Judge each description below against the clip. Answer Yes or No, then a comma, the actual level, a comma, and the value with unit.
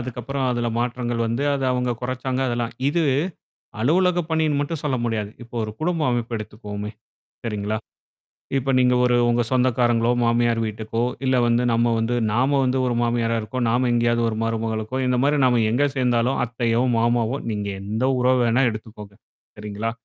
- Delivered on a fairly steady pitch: Yes, narrow, 2.0 semitones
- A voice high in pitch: No, low, 120 Hz